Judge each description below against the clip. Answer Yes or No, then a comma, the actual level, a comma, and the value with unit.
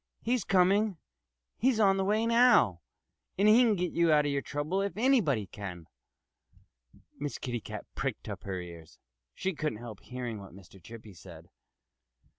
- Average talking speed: Yes, average, 165 wpm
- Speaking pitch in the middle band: Yes, medium, 150 Hz